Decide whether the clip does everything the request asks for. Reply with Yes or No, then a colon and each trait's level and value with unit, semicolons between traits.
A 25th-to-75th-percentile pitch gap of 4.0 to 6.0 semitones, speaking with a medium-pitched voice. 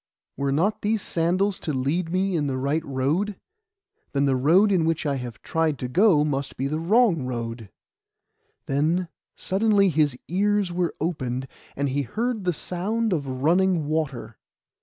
Yes: wide, 5.4 semitones; medium, 160 Hz